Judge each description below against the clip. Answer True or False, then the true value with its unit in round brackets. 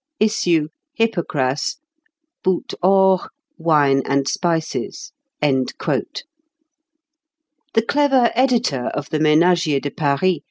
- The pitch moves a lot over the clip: False (5.0 semitones)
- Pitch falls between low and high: True (165 Hz)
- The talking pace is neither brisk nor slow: False (90 wpm)